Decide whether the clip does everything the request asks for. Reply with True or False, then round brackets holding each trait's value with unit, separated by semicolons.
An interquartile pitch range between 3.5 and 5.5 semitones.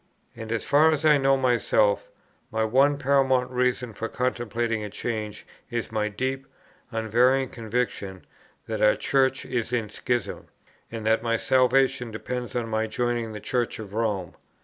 False (2.8 semitones)